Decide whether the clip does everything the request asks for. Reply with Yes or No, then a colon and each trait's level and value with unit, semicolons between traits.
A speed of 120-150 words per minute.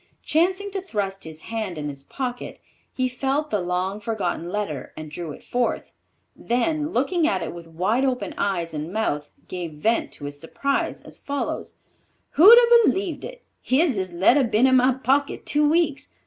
No: average, 175 wpm